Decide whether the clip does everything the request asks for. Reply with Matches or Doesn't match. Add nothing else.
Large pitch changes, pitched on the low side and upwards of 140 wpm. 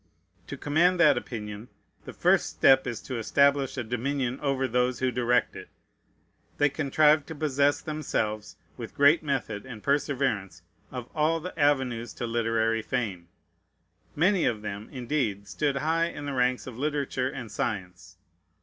Doesn't match